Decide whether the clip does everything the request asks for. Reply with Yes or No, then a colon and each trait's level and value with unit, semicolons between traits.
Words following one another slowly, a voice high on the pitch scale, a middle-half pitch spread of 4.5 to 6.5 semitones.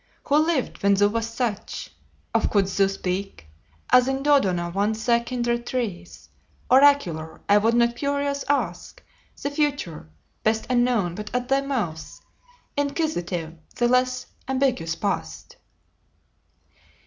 Yes: slow, 125 wpm; high, 235 Hz; wide, 5.6 semitones